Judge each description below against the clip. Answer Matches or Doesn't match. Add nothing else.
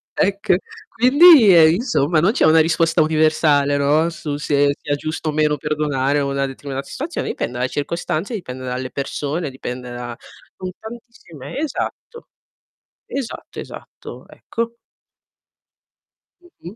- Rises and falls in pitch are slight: Doesn't match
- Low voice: Doesn't match